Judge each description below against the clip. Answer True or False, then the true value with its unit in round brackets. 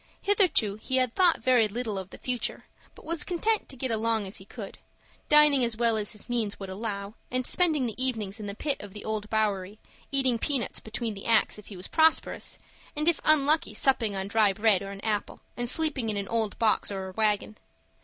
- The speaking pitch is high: True (225 Hz)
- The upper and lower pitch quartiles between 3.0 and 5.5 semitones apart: True (4.2 semitones)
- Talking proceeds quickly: True (215 wpm)